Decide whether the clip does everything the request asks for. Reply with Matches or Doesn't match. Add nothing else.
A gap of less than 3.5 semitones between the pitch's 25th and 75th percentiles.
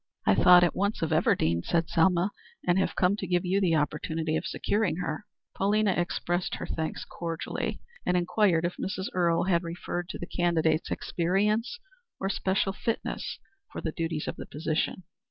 Matches